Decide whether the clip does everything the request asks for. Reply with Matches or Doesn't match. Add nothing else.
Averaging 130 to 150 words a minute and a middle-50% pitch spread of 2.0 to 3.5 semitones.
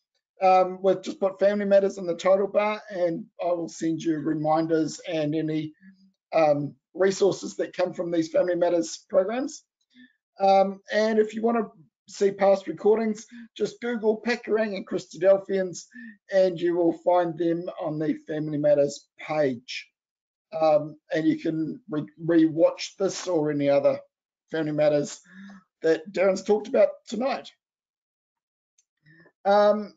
Doesn't match